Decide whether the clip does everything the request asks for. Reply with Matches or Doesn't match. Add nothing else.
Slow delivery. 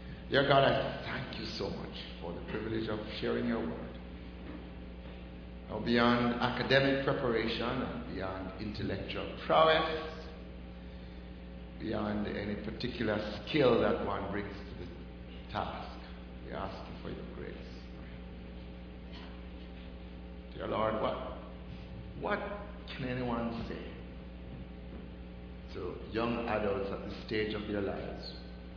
Matches